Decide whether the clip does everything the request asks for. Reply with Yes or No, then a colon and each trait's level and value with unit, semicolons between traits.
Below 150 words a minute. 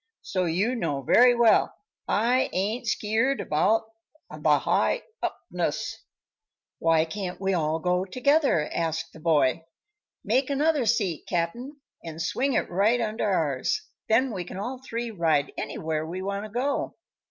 Yes: average, 140 wpm